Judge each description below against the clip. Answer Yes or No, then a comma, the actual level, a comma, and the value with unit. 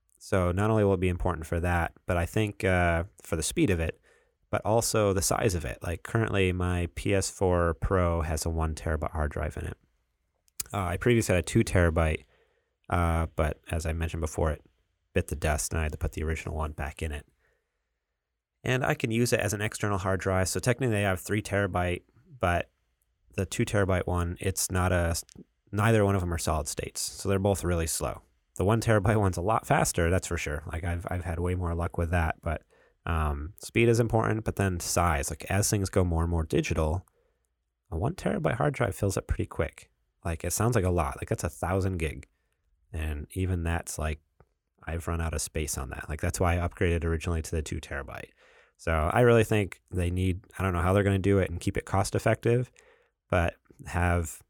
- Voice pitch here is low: Yes, very low, 90 Hz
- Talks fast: Yes, fast, 220 wpm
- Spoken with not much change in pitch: No, average, 3.3 semitones